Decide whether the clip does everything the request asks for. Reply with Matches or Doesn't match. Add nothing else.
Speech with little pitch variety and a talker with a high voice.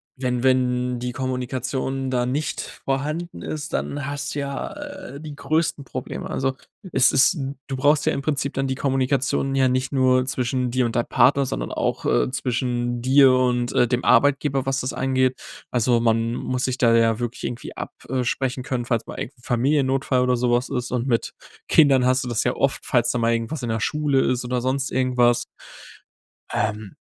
Doesn't match